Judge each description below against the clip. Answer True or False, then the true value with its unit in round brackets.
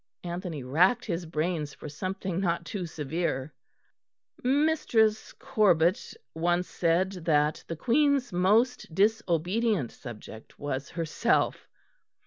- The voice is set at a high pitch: False (175 Hz)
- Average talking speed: False (105 wpm)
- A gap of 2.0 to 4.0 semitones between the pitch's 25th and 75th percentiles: False (5.2 semitones)